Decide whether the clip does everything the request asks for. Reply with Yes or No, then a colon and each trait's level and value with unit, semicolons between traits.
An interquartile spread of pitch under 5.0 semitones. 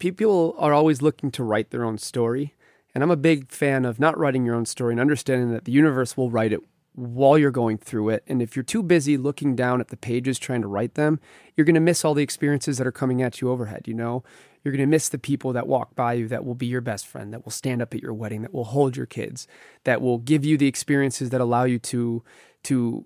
Yes: average, 3.5 semitones